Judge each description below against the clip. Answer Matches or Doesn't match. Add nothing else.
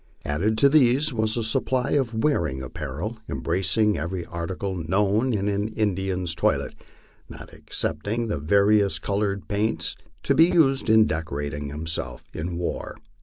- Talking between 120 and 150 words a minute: Matches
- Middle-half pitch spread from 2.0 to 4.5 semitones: Doesn't match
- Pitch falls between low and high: Doesn't match